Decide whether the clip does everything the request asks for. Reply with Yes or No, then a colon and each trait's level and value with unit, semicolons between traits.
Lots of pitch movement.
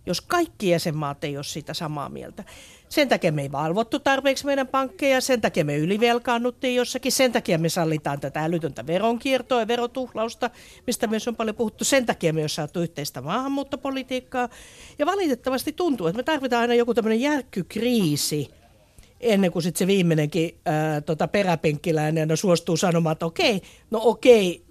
Yes: wide, 7.5 semitones